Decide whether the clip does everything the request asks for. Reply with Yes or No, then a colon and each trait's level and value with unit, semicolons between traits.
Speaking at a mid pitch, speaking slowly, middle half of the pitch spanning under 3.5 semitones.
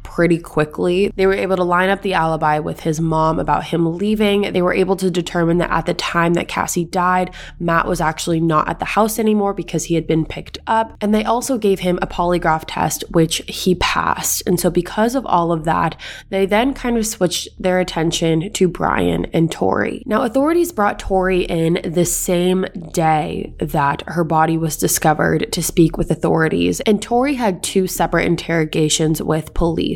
No: medium, 175 Hz; average, 190 wpm; average, 3.0 semitones